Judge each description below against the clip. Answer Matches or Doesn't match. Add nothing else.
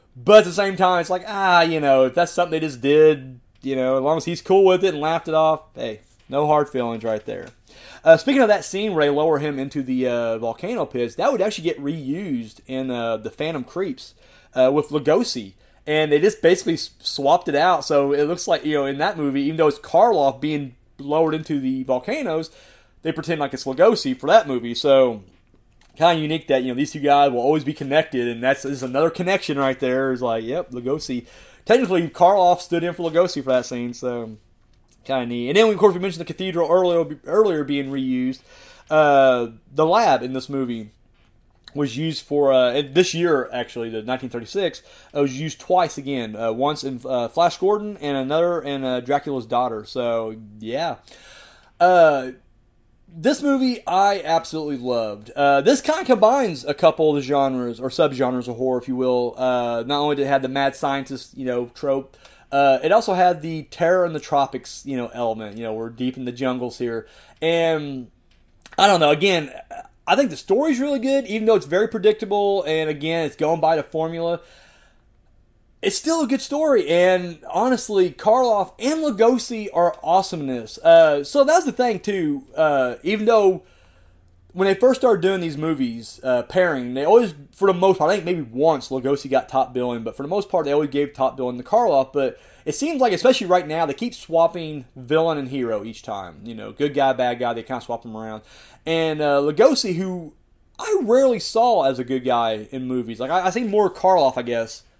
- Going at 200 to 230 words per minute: Matches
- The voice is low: Doesn't match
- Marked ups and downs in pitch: Matches